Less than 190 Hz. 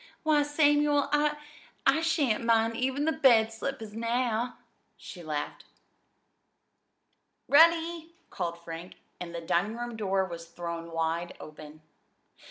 No: high, 225 Hz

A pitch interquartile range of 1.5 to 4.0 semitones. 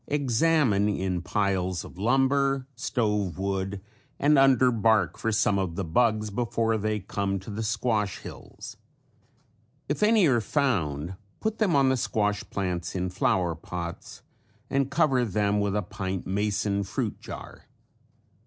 No: average, 4.9 semitones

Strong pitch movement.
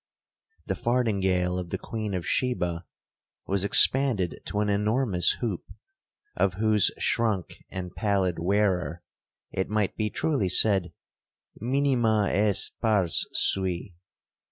No: average, 3.2 semitones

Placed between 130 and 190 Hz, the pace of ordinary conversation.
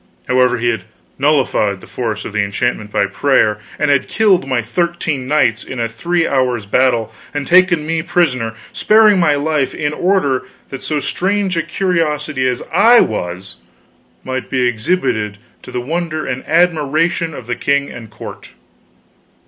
Yes: medium, 140 Hz; average, 165 wpm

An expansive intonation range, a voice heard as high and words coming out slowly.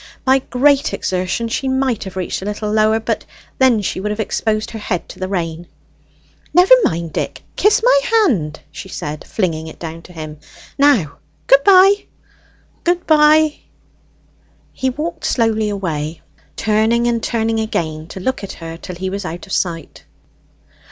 No: wide, 7.1 semitones; high, 215 Hz; average, 165 wpm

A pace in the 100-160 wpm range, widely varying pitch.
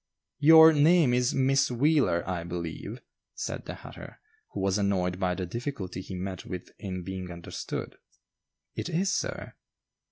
Yes: average, 150 wpm; wide, 7.5 semitones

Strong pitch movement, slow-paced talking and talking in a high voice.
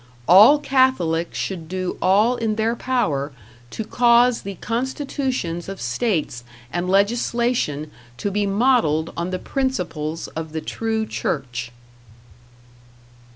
Yes: wide, 6.6 semitones; slow, 115 wpm; high, 200 Hz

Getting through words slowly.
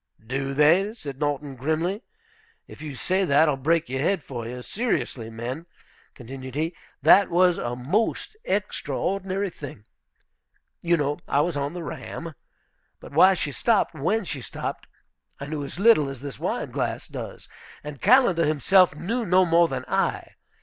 No: average, 160 wpm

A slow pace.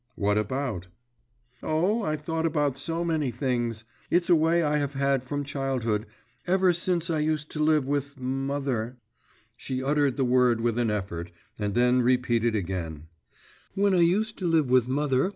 No: average, 170 wpm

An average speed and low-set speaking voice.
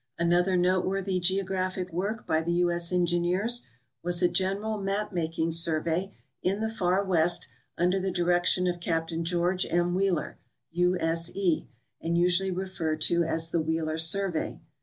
No: average, 160 wpm; medium, 175 Hz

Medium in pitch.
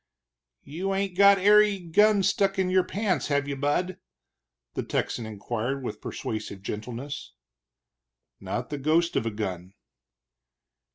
Yes: medium, 150 Hz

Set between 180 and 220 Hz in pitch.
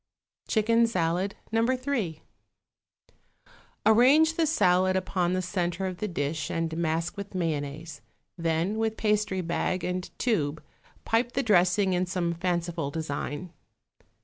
Yes: medium, 185 Hz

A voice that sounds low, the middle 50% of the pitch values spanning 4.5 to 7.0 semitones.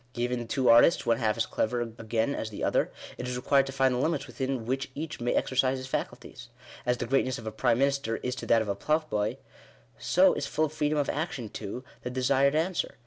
No: low, 125 Hz; average, 3.1 semitones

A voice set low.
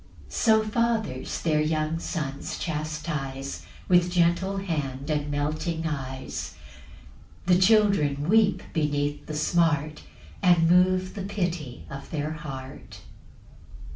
No: medium, 155 Hz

